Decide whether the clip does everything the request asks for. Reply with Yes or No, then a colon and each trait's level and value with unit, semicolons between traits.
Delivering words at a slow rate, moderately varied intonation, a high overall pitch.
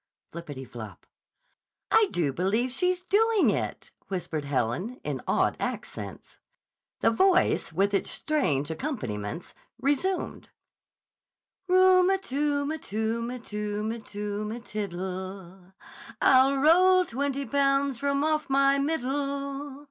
No: slow, 120 wpm; wide, 7.2 semitones; very high, 260 Hz